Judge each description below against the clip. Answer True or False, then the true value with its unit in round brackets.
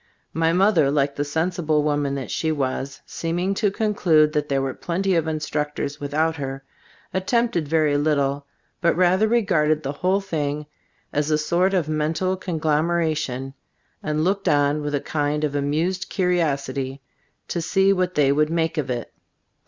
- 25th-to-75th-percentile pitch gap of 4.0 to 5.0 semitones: False (3.4 semitones)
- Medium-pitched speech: True (155 Hz)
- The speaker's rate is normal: True (165 wpm)